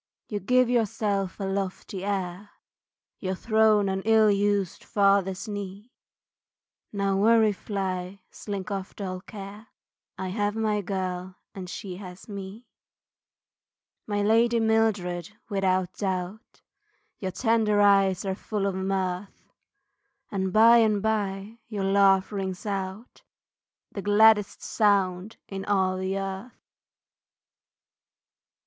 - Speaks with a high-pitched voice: Yes, high, 200 Hz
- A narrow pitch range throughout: Yes, narrow, 1.9 semitones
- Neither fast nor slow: No, slow, 115 wpm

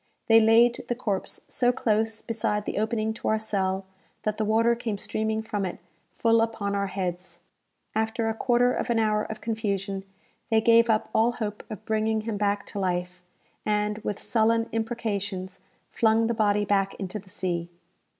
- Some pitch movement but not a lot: No, narrow, 2.0 semitones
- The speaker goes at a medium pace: Yes, average, 175 wpm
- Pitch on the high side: Yes, high, 215 Hz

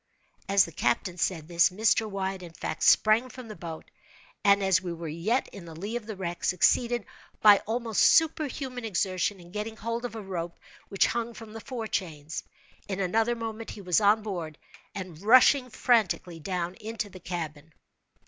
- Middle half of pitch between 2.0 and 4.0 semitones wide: No, average, 4.4 semitones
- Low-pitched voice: No, high, 200 Hz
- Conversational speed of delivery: Yes, average, 180 wpm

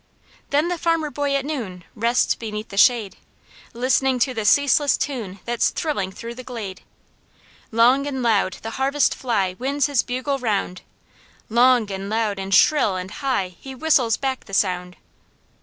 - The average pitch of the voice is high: Yes, high, 240 Hz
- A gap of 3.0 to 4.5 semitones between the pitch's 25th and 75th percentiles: No, average, 5.3 semitones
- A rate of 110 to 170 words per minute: Yes, average, 160 wpm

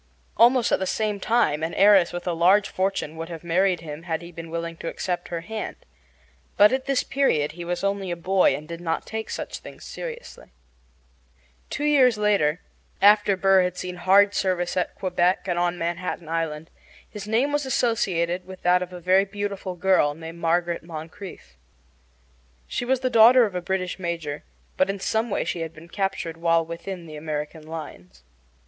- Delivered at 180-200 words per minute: Yes, average, 185 wpm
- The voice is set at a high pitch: No, medium, 180 Hz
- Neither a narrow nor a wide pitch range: Yes, average, 3.3 semitones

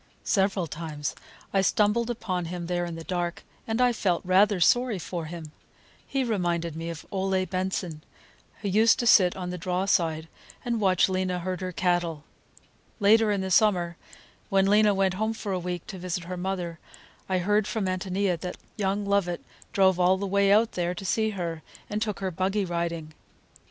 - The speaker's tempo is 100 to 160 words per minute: No, average, 185 wpm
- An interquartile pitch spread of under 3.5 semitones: Yes, narrow, 2.6 semitones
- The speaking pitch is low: No, medium, 185 Hz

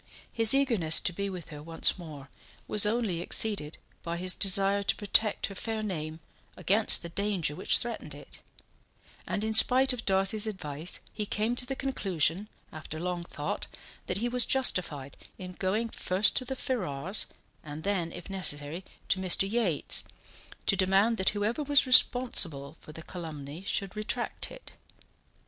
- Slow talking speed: No, average, 160 wpm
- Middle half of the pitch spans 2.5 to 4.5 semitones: No, average, 5.0 semitones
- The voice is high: Yes, high, 195 Hz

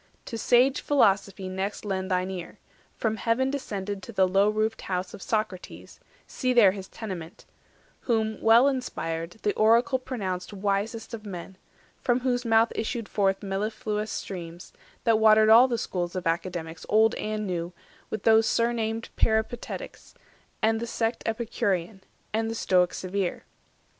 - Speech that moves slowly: No, average, 145 wpm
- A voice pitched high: Yes, high, 215 Hz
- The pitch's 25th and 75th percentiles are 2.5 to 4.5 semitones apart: Yes, average, 3.2 semitones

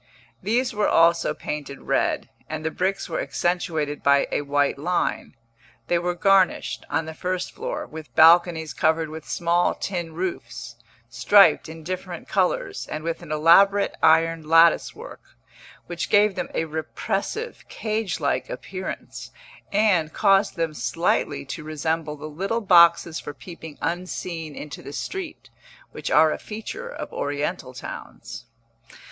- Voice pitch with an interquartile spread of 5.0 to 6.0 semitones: No, average, 3.4 semitones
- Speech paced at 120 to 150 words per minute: Yes, average, 140 wpm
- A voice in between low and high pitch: Yes, medium, 165 Hz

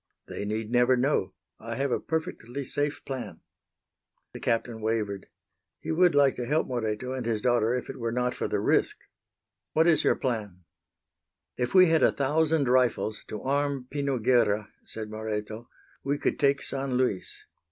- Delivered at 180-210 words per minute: No, average, 170 wpm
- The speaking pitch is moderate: No, low, 125 Hz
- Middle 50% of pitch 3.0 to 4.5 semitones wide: Yes, average, 4.2 semitones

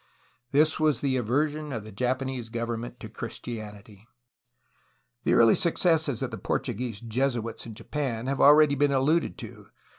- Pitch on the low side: Yes, low, 125 Hz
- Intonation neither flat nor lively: Yes, average, 4.0 semitones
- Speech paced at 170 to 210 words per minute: No, average, 145 wpm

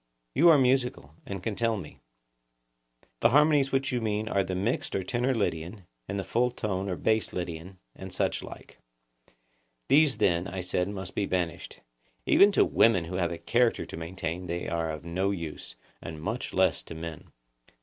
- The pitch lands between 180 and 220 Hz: No, very low, 95 Hz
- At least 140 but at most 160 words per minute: No, average, 180 wpm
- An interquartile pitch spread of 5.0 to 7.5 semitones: Yes, wide, 5.6 semitones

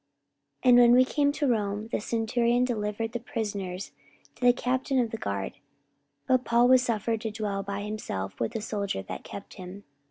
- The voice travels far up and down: No, average, 3.4 semitones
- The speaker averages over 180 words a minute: Yes, average, 190 wpm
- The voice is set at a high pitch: Yes, high, 225 Hz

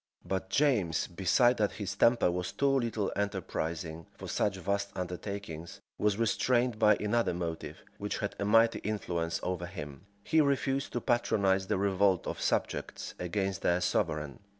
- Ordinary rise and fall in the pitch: Yes, average, 4.3 semitones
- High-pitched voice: No, low, 100 Hz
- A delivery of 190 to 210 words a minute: No, average, 150 wpm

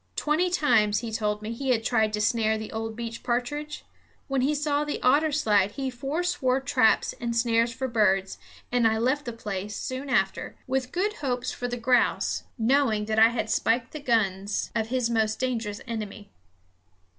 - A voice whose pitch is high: Yes, high, 235 Hz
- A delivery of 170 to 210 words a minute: Yes, average, 180 wpm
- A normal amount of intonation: Yes, average, 3.4 semitones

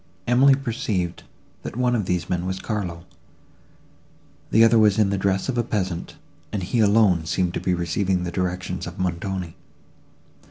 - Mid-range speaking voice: No, very low, 95 Hz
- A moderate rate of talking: Yes, average, 165 wpm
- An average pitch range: Yes, average, 3.6 semitones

